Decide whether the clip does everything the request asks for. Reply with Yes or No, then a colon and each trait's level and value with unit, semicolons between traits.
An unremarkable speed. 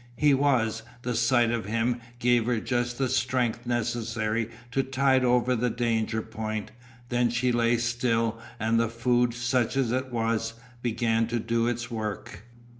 Yes: average, 160 wpm